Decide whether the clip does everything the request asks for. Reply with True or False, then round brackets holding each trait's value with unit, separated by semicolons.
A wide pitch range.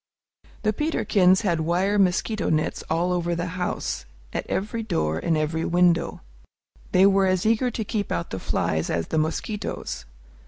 False (3.8 semitones)